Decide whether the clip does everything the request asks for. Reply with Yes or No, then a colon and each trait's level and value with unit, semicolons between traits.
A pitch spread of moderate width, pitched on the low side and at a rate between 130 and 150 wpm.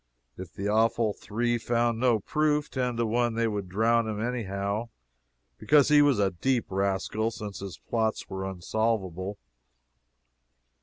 Yes: average, 3.2 semitones; low, 110 Hz; average, 145 wpm